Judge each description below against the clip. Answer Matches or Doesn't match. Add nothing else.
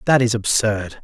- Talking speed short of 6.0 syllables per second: Matches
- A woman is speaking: Doesn't match